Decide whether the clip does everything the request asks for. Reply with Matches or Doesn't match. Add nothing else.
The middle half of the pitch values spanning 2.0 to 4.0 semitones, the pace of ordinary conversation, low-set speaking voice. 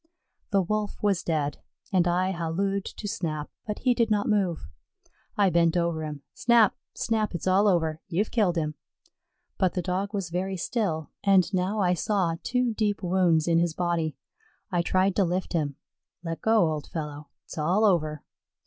Doesn't match